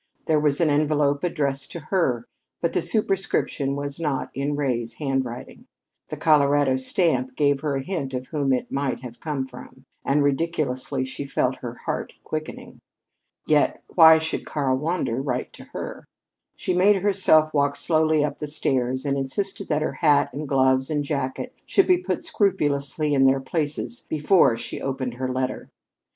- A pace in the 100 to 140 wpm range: No, average, 165 wpm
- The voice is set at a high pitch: No, medium, 145 Hz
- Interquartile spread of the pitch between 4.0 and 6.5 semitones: No, average, 2.9 semitones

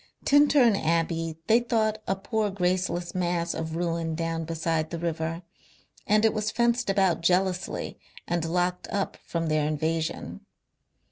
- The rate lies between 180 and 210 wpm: No, average, 140 wpm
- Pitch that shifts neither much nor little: Yes, average, 3.6 semitones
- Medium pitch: Yes, medium, 175 Hz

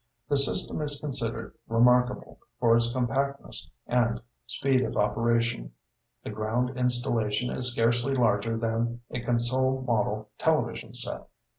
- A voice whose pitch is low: Yes, low, 120 Hz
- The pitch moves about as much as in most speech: No, narrow, 2.0 semitones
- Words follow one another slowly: Yes, slow, 125 wpm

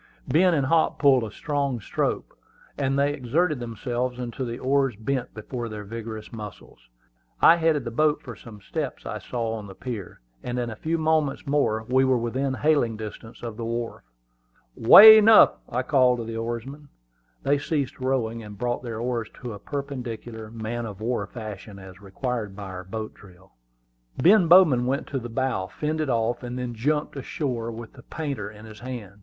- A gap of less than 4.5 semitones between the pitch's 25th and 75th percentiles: Yes, average, 3.9 semitones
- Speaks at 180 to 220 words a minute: Yes, average, 185 wpm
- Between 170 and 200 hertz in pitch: No, low, 120 Hz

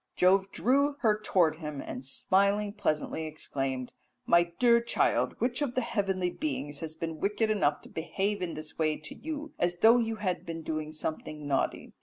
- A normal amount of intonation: No, wide, 5.9 semitones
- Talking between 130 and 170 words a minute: No, average, 180 wpm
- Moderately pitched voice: Yes, medium, 180 Hz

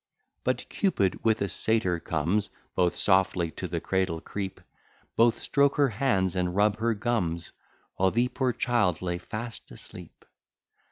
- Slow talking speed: No, average, 150 wpm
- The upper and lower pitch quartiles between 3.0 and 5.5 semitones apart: Yes, average, 4.4 semitones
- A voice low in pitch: Yes, low, 100 Hz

